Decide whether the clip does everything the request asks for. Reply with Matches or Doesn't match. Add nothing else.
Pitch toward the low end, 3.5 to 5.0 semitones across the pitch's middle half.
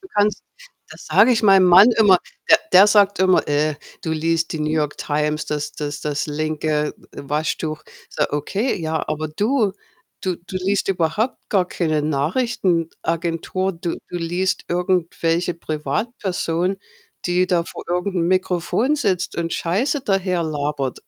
Doesn't match